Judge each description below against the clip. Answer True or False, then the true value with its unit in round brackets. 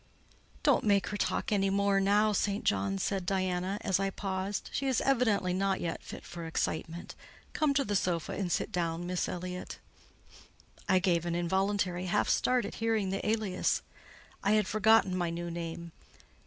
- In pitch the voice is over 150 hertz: True (190 Hz)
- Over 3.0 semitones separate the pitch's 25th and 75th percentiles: False (2.7 semitones)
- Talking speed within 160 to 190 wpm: True (175 wpm)